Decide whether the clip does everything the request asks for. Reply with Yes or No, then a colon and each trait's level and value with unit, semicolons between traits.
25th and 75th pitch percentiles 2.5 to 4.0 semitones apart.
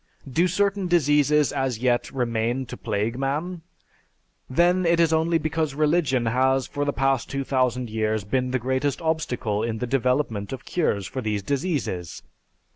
No: average, 4.7 semitones